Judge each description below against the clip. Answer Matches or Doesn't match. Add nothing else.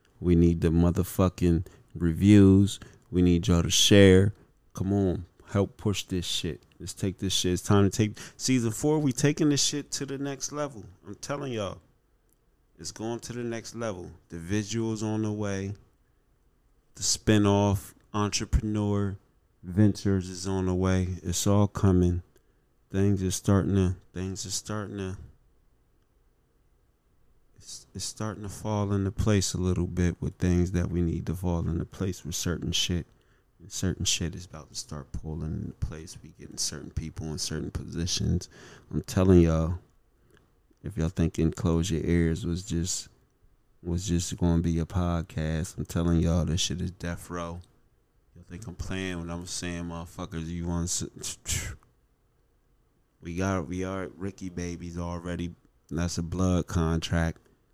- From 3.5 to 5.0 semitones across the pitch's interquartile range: Doesn't match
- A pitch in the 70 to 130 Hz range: Matches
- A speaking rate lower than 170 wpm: Matches